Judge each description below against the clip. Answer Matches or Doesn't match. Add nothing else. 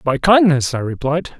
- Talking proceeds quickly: Doesn't match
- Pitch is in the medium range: Matches